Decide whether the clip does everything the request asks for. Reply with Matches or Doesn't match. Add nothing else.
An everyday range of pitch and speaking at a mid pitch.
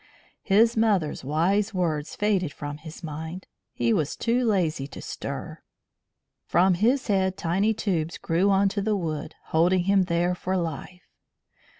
Matches